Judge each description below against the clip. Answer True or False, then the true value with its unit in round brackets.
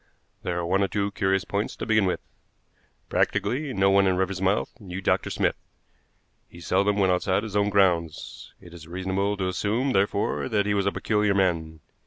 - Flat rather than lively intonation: True (1.8 semitones)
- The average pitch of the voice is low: True (95 Hz)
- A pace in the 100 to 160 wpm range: False (185 wpm)